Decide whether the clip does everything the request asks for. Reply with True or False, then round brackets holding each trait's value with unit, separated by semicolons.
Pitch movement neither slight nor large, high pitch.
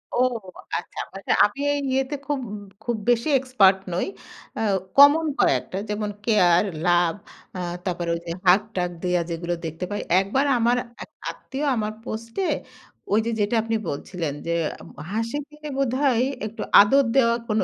False (6.1 semitones; 220 Hz)